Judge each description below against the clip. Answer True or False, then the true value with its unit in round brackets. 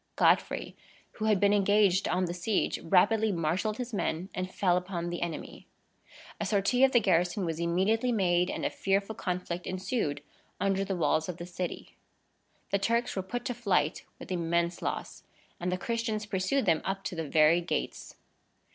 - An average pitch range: True (3.3 semitones)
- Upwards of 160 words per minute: True (175 wpm)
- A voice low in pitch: False (185 Hz)